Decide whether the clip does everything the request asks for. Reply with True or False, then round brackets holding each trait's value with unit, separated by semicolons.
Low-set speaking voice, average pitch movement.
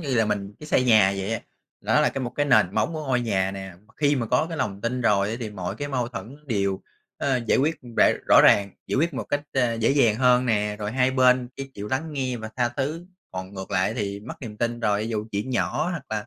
True (115 Hz; 4.2 semitones)